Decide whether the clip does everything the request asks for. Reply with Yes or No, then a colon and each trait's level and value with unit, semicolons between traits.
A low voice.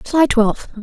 No: high, 245 Hz